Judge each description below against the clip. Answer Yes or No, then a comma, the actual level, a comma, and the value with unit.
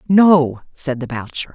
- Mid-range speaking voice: Yes, medium, 145 Hz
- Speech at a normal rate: Yes, average, 155 wpm